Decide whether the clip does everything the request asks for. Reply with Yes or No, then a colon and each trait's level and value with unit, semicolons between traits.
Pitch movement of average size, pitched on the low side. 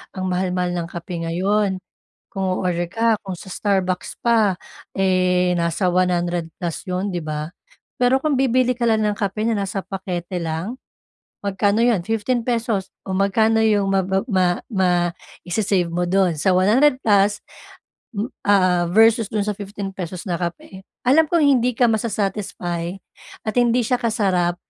No: average, 3.6 semitones; high, 195 Hz